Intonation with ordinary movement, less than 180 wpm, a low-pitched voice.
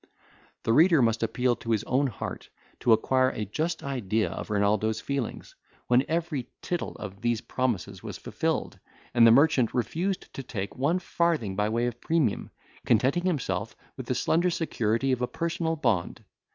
No: wide, 6.3 semitones; average, 165 wpm; low, 125 Hz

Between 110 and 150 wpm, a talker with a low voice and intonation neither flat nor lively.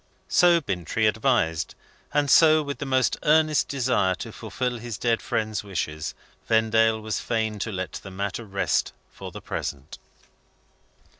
Yes: average, 145 wpm; low, 110 Hz; average, 4.8 semitones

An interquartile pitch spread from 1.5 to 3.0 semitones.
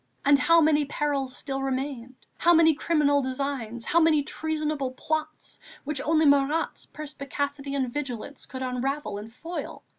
Yes: average, 2.7 semitones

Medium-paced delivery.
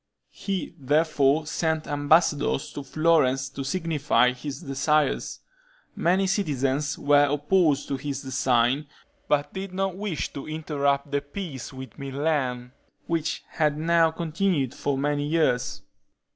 No: slow, 125 wpm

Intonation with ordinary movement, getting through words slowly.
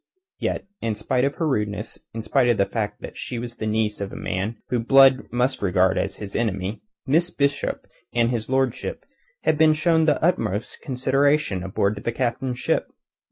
No: average, 4.4 semitones; average, 185 wpm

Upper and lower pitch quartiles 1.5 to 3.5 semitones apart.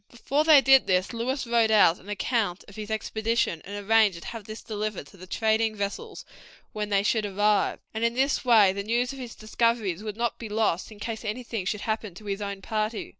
Yes: narrow, 2.4 semitones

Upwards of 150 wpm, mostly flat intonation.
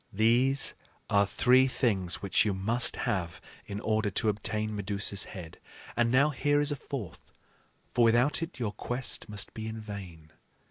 No: average, 165 wpm; average, 3.7 semitones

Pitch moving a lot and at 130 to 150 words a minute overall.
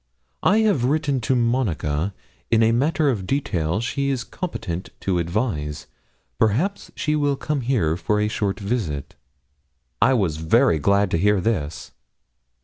Yes: wide, 7.5 semitones; average, 145 wpm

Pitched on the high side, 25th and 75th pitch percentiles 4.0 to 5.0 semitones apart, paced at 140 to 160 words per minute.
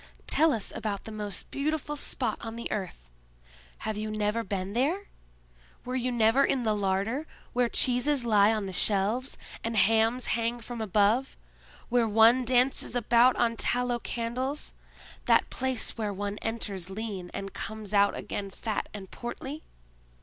No: high, 225 Hz; average, 3.2 semitones; average, 155 wpm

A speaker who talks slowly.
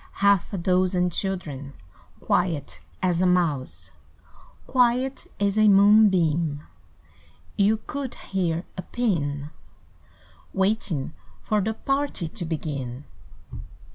Yes: slow, 100 wpm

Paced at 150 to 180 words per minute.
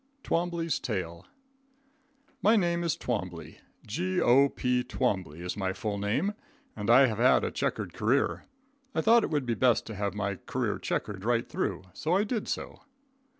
Yes: average, 160 wpm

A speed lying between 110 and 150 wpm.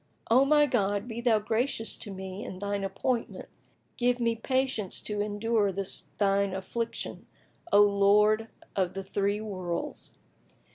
Yes: average, 145 wpm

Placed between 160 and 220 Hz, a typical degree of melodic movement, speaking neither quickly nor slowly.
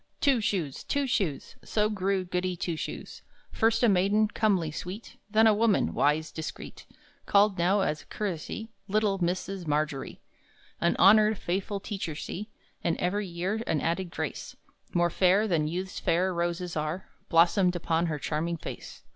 Yes: medium, 185 Hz; average, 3.6 semitones; average, 155 wpm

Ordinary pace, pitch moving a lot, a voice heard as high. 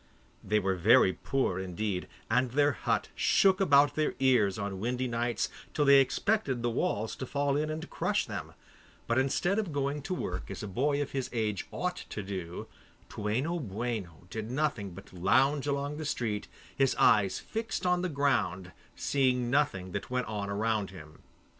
No: average, 175 wpm; wide, 6.0 semitones; low, 125 Hz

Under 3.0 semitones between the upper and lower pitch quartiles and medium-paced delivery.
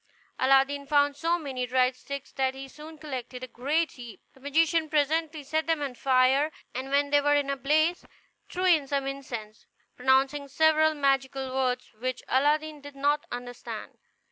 Yes: narrow, 2.5 semitones; average, 170 wpm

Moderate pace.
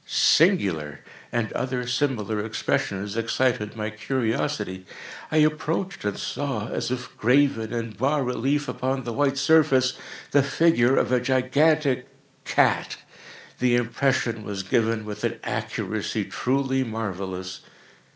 No: slow, 120 wpm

